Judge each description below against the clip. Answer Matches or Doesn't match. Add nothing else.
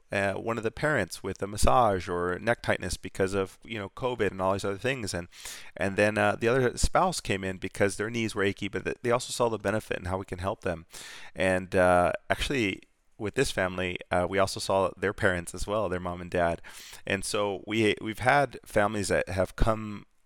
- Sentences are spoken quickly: Matches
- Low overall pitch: Matches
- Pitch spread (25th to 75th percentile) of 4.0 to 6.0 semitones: Doesn't match